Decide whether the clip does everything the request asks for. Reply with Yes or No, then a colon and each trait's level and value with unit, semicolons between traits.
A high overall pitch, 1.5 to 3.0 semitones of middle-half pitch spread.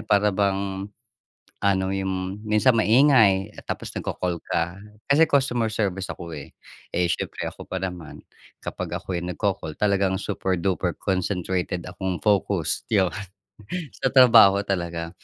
No: very low, 95 Hz; narrow, 2.6 semitones